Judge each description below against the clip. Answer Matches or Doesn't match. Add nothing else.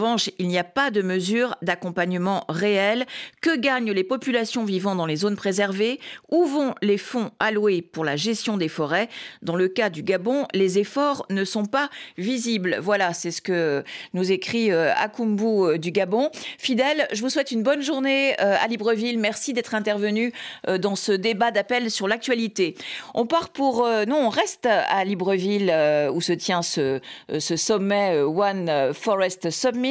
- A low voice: Doesn't match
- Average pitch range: Matches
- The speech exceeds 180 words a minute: Doesn't match